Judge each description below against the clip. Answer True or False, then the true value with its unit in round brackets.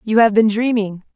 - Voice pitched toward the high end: True (215 Hz)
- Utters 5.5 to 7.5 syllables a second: False (5.2 syllables/s)